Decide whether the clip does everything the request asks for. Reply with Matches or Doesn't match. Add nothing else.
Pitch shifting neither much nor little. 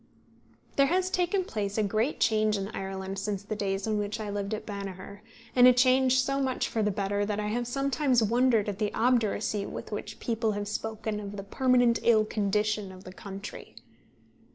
Matches